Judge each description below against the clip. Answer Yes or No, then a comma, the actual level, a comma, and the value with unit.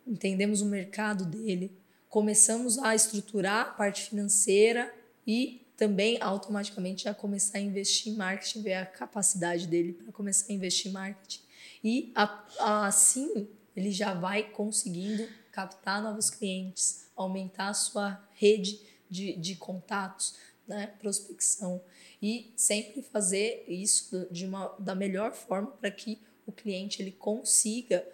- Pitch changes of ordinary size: No, narrow, 2.0 semitones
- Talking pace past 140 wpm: No, average, 135 wpm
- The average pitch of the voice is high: Yes, high, 205 Hz